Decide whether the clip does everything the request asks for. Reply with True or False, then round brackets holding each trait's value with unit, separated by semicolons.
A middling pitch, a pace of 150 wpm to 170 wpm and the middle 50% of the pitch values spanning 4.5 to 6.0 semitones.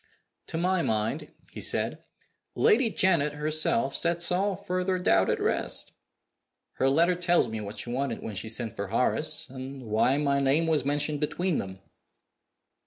True (150 Hz; 160 wpm; 5.4 semitones)